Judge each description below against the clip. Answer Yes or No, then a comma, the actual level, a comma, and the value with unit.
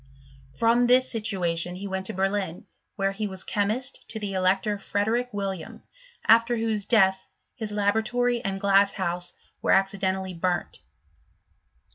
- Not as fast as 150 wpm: Yes, slow, 135 wpm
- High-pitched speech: Yes, high, 200 Hz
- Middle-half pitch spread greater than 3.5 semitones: No, average, 2.7 semitones